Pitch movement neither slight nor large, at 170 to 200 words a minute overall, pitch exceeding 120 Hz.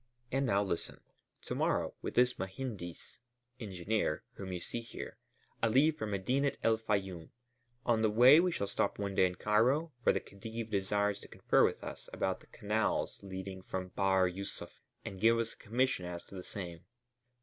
No: average, 3.5 semitones; average, 180 wpm; low, 100 Hz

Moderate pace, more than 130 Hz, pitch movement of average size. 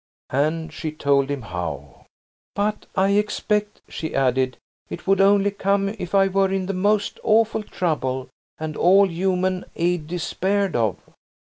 Yes: average, 145 wpm; medium, 185 Hz; average, 5.0 semitones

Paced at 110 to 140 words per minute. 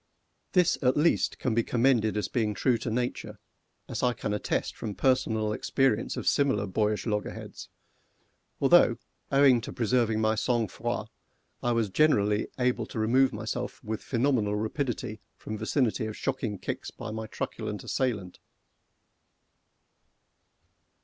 Yes: slow, 135 wpm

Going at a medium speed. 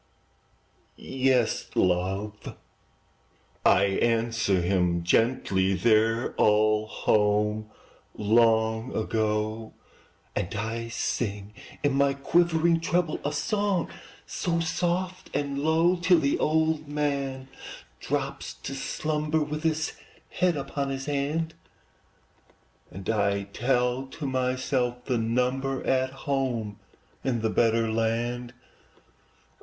No: slow, 100 wpm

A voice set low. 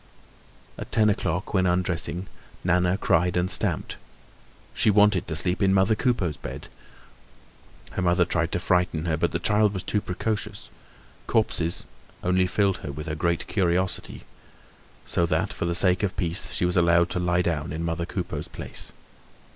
Yes: very low, 90 Hz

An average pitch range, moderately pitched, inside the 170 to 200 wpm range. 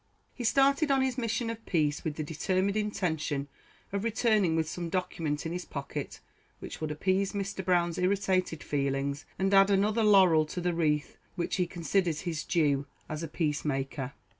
Yes: average, 4.5 semitones; medium, 175 Hz; average, 175 wpm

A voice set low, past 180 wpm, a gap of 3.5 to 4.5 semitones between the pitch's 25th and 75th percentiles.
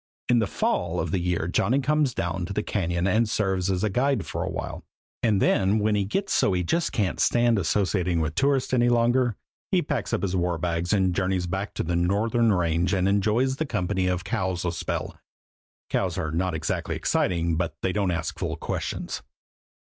Yes: very low, 95 Hz; average, 195 wpm; average, 4.0 semitones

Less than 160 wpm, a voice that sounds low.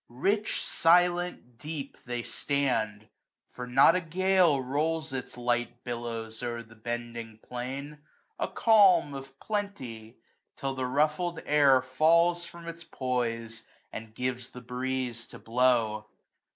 Yes: slow, 135 wpm; low, 130 Hz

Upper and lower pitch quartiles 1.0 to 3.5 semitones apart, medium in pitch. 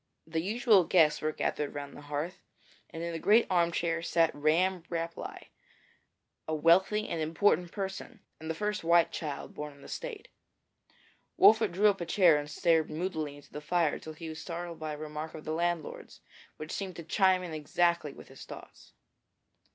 Yes: average, 2.9 semitones; medium, 165 Hz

